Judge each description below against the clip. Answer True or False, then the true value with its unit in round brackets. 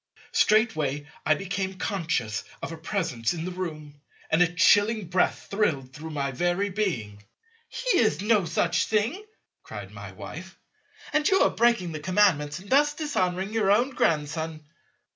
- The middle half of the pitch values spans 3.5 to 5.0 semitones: False (5.5 semitones)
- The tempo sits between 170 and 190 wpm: False (155 wpm)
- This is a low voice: False (180 Hz)